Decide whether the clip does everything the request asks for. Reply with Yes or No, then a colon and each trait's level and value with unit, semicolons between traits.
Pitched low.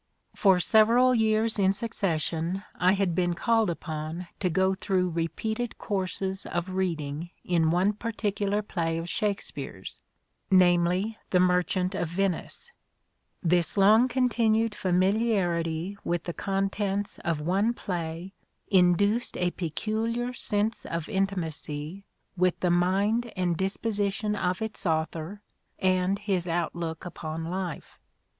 No: medium, 185 Hz